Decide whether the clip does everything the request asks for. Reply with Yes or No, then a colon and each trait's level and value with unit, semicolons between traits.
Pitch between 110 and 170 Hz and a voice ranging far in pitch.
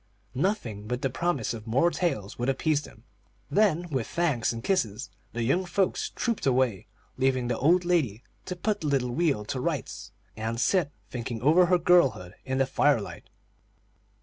Yes: low, 135 Hz; wide, 6.7 semitones